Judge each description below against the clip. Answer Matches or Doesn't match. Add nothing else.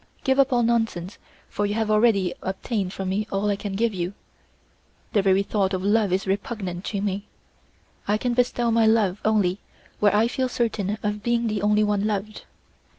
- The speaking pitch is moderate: Doesn't match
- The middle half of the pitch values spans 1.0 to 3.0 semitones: Matches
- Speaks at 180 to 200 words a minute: Matches